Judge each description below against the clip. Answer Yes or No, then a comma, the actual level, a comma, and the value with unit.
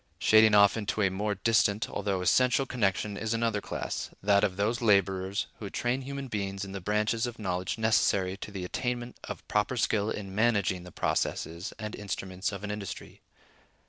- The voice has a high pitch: No, low, 105 Hz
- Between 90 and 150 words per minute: No, average, 175 wpm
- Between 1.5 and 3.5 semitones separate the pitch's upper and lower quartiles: Yes, narrow, 2.5 semitones